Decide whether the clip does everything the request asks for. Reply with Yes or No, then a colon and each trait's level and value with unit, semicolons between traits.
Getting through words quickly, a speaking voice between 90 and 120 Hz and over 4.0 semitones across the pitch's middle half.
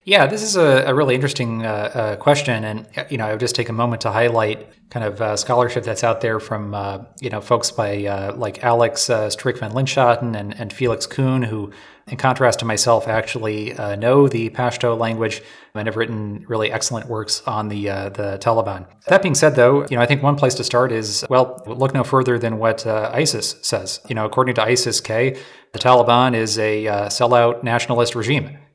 No: fast, 215 wpm; low, 115 Hz; narrow, 2.6 semitones